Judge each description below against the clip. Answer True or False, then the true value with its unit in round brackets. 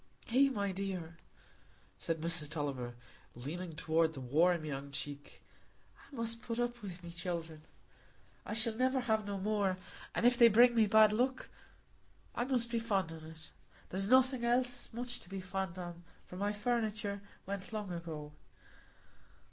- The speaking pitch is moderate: False (195 Hz)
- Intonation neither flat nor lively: False (5.8 semitones)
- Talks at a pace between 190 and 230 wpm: False (155 wpm)